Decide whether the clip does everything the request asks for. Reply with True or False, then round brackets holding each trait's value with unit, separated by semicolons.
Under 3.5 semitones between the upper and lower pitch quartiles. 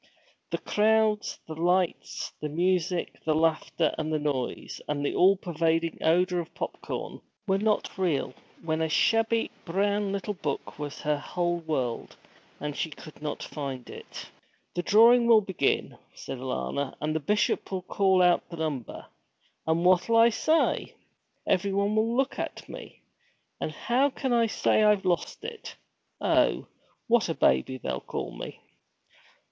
False (5.2 semitones)